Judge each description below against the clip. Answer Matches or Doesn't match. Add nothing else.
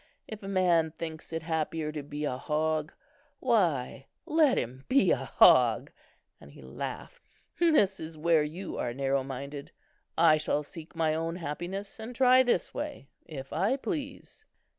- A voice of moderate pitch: Matches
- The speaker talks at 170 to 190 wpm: Doesn't match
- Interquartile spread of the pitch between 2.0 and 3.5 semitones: Doesn't match